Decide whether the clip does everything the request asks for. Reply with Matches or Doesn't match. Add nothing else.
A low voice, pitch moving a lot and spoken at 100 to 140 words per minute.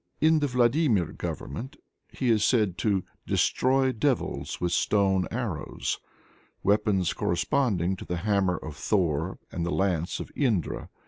Matches